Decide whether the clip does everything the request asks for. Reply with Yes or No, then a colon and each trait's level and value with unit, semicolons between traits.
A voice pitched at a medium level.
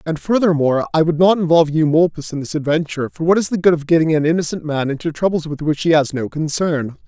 Yes: medium, 160 Hz